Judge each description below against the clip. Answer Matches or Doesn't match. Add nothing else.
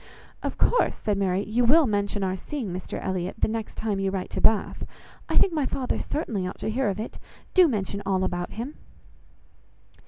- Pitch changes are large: Doesn't match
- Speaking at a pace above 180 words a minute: Matches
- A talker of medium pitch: Doesn't match